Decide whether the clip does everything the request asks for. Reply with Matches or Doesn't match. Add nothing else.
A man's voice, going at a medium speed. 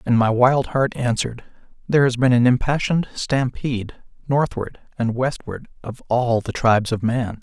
Matches